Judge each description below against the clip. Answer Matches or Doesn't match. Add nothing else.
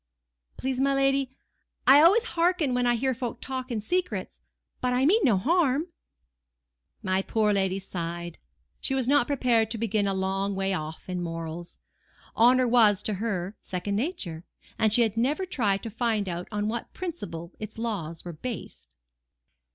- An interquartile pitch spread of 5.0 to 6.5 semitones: Matches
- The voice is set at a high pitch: Matches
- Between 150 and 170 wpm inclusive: Matches